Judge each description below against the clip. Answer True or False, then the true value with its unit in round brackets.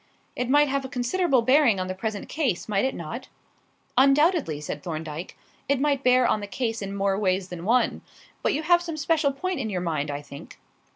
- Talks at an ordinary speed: False (210 wpm)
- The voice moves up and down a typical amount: False (7.2 semitones)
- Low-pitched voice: False (240 Hz)